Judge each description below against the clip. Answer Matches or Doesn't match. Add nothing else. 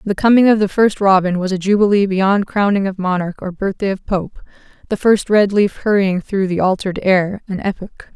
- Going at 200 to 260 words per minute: Matches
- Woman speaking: Matches